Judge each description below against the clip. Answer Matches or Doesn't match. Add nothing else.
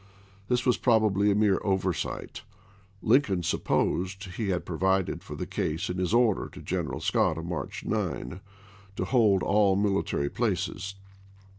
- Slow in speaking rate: Doesn't match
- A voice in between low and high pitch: Doesn't match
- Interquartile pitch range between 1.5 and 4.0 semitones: Matches